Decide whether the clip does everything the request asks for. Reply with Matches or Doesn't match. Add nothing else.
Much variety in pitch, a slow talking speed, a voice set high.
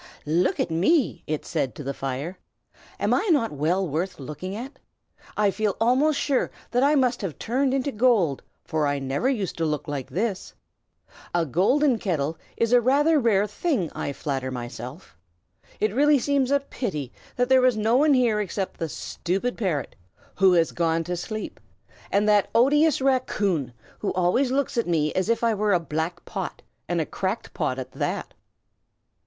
Doesn't match